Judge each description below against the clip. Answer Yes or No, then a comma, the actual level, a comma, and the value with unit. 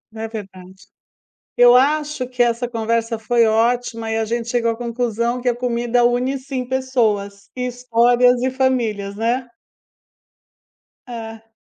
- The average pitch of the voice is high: Yes, high, 240 Hz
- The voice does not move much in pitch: Yes, narrow, 1.9 semitones